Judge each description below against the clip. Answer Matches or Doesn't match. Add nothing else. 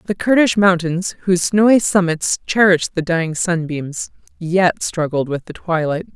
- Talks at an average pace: Matches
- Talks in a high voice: Doesn't match